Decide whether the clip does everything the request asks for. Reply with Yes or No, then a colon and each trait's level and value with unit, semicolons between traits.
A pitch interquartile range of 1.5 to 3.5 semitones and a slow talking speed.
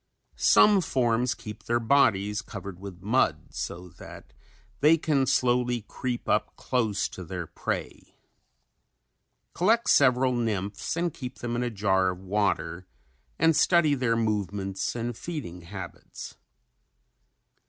No: average, 5.0 semitones; slow, 125 wpm